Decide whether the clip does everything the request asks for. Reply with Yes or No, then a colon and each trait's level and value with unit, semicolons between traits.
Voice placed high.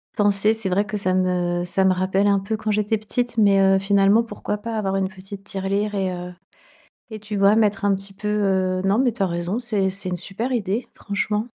Yes: high, 200 Hz